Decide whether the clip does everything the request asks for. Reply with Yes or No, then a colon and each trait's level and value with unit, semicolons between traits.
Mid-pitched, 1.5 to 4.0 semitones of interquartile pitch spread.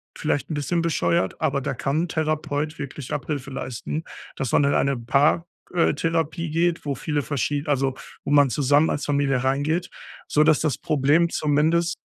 Yes: medium, 145 Hz; narrow, 2.5 semitones